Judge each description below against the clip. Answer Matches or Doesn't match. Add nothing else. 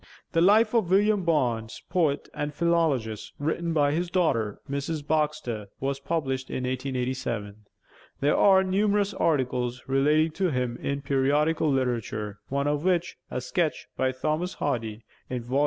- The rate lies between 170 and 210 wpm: Doesn't match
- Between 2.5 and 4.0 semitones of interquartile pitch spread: Doesn't match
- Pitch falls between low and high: Matches